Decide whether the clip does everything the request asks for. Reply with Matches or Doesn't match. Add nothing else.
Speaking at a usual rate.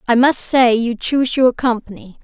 Matches